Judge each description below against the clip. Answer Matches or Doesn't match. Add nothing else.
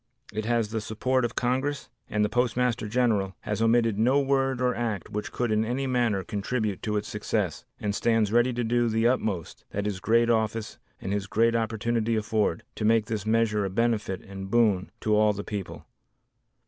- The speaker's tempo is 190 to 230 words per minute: Matches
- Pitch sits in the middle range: Doesn't match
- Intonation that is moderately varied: Doesn't match